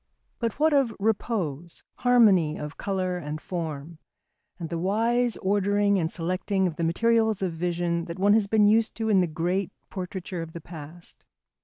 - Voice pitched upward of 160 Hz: Yes, medium, 185 Hz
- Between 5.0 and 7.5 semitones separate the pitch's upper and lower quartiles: No, average, 4.1 semitones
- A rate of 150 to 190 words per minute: Yes, average, 170 wpm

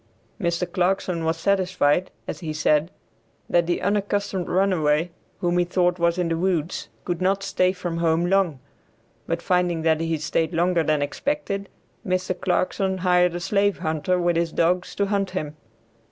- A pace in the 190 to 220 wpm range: No, average, 165 wpm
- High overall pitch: No, medium, 175 Hz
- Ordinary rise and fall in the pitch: No, narrow, 2.2 semitones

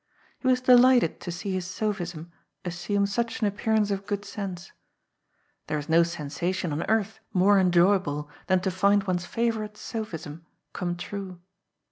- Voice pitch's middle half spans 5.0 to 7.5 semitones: No, average, 3.3 semitones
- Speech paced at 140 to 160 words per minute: Yes, average, 150 wpm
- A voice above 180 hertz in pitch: Yes, high, 190 Hz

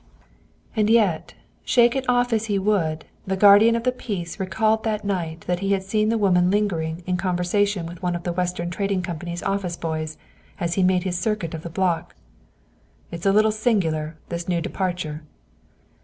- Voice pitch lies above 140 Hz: Yes, medium, 185 Hz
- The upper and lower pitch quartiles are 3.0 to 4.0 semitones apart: Yes, average, 3.5 semitones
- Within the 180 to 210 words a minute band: Yes, average, 185 wpm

